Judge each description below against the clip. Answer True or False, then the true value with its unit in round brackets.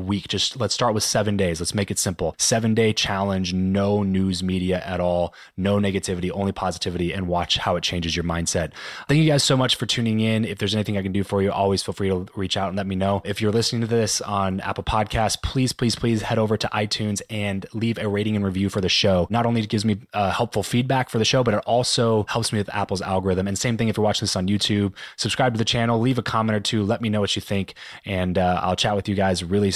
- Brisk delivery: True (265 wpm)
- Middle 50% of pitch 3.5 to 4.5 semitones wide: False (2.8 semitones)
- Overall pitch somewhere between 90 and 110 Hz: True (100 Hz)